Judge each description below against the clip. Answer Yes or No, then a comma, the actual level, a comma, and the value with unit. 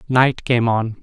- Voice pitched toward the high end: No, low, 120 Hz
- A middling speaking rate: Yes, average, 175 wpm